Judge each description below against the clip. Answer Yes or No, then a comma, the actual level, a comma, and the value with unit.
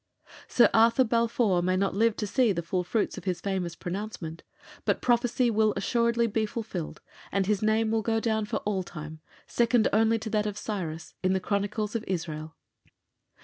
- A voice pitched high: Yes, high, 210 Hz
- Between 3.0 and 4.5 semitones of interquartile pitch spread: Yes, average, 3.4 semitones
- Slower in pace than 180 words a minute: No, average, 185 wpm